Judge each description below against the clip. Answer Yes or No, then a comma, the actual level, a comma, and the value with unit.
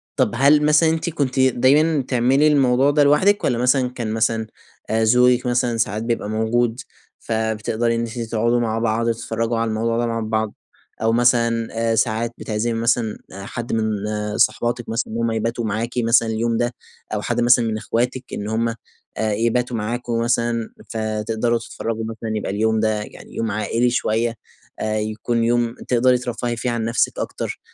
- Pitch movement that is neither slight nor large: No, narrow, 1.6 semitones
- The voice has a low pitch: Yes, low, 115 Hz